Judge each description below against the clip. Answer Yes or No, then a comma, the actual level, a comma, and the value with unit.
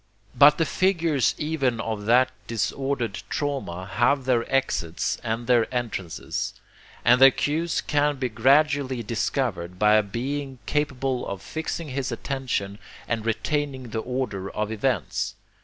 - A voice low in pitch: Yes, low, 125 Hz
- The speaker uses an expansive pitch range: No, average, 4.1 semitones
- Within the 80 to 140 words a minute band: Yes, slow, 135 wpm